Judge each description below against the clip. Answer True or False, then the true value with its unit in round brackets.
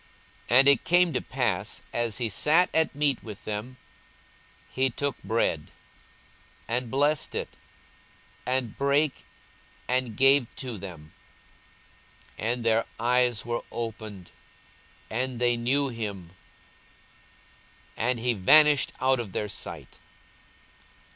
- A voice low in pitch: True (120 Hz)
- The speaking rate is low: True (120 wpm)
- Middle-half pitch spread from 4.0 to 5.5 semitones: False (3.3 semitones)